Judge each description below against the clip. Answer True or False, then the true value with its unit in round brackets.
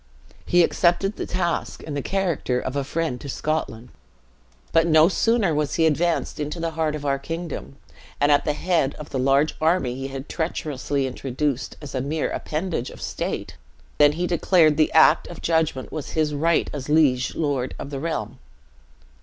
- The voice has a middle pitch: True (150 Hz)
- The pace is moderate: True (180 wpm)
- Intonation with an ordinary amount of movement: True (3.1 semitones)